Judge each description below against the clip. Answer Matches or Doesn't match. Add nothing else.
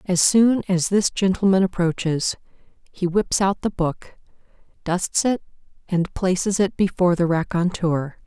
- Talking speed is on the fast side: Doesn't match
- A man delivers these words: Doesn't match